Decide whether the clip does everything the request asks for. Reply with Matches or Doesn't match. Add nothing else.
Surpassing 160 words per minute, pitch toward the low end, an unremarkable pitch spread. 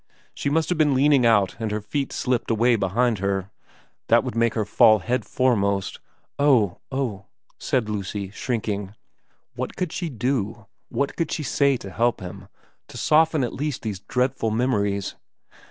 Matches